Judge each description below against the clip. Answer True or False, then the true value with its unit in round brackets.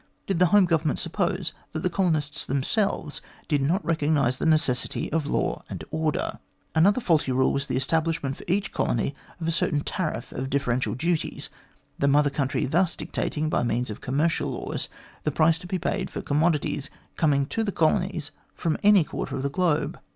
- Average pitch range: True (3.4 semitones)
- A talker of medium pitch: True (155 Hz)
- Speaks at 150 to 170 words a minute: False (185 wpm)